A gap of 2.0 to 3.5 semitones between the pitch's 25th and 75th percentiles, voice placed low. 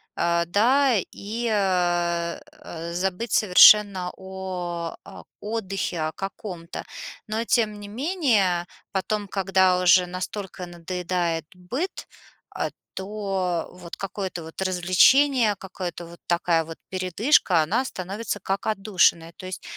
No: average, 3.2 semitones; high, 190 Hz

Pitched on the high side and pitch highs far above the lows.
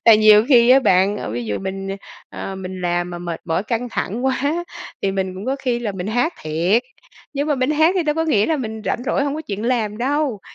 Yes: high, 220 Hz; wide, 5.8 semitones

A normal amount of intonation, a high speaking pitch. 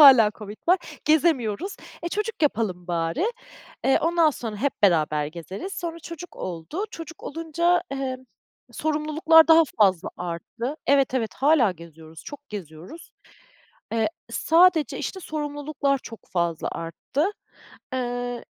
No: wide, 8.8 semitones; very high, 270 Hz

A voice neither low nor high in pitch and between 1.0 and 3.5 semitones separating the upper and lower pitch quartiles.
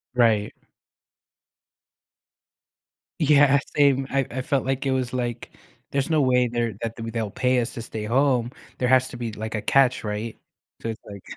No: low, 125 Hz; average, 2.8 semitones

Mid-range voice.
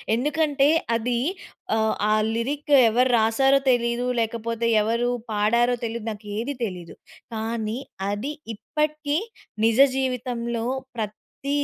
No: high, 235 Hz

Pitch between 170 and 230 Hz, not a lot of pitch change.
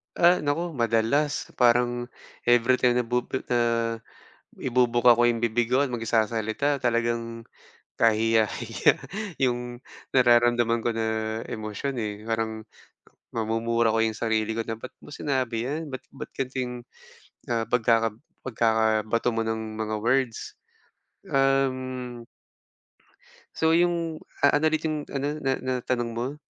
No: low, 120 Hz; narrow, 2.3 semitones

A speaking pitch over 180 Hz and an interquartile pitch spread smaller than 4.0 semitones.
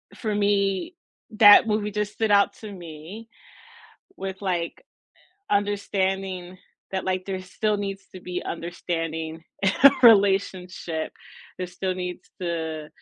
Yes: high, 190 Hz; narrow, 2.5 semitones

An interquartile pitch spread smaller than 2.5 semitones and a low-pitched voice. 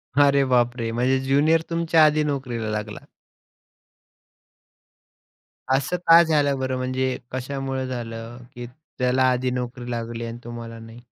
No: average, 2.8 semitones; low, 130 Hz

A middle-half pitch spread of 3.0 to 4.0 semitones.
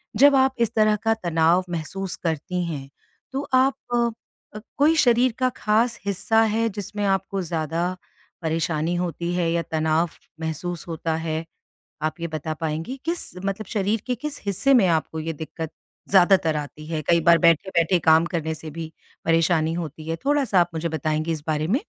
No: average, 4.8 semitones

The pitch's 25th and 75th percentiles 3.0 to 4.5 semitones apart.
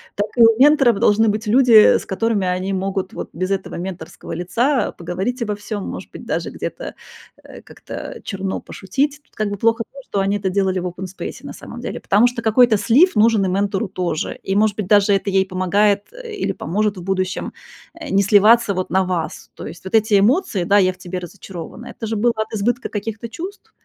Yes: average, 3.3 semitones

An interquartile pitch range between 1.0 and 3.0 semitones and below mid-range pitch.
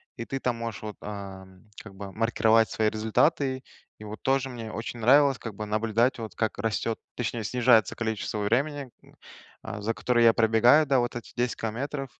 Yes: narrow, 2.6 semitones; low, 115 Hz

